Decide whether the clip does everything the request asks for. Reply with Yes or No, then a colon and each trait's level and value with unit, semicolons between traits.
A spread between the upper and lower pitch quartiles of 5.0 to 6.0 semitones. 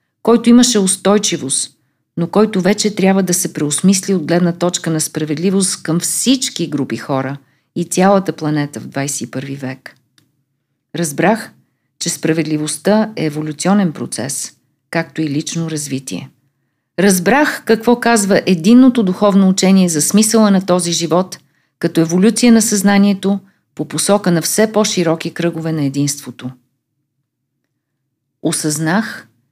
Yes: wide, 5.5 semitones